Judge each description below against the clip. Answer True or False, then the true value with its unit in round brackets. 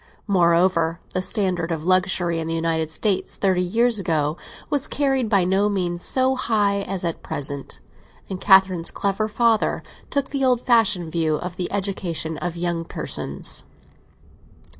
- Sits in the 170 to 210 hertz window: True (185 Hz)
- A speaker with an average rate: True (150 wpm)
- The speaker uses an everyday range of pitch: True (3.8 semitones)